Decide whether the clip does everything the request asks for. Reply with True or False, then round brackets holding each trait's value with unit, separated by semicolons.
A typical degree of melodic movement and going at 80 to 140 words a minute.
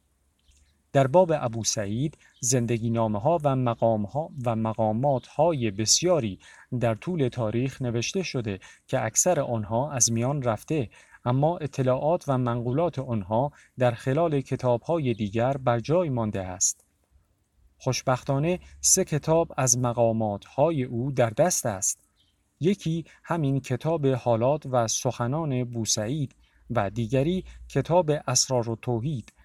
True (4.3 semitones; 125 wpm)